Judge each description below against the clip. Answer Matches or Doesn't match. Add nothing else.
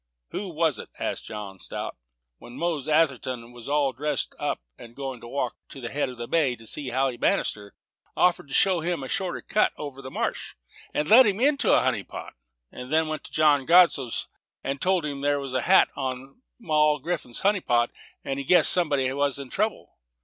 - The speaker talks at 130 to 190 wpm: Doesn't match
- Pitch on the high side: Doesn't match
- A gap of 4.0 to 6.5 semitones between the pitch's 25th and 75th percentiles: Matches